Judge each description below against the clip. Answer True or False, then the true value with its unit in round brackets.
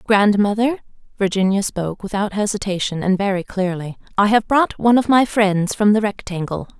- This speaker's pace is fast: False (160 wpm)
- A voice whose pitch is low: False (205 Hz)